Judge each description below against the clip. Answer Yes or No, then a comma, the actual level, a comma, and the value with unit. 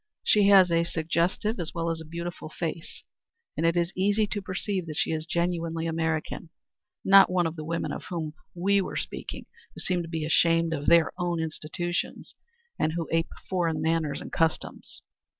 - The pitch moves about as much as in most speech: No, narrow, 1.7 semitones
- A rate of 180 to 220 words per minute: Yes, average, 185 wpm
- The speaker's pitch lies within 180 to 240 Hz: No, medium, 170 Hz